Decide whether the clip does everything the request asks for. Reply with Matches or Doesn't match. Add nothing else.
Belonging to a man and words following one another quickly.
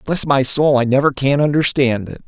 Matches